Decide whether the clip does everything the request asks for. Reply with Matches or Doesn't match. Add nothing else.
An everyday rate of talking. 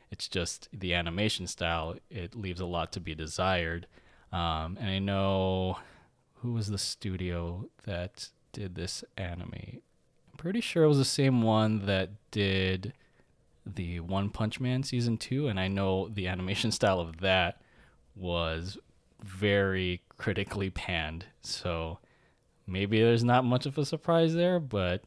Matches